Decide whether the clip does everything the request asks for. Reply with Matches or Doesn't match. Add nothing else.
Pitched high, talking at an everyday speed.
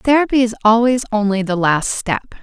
Matches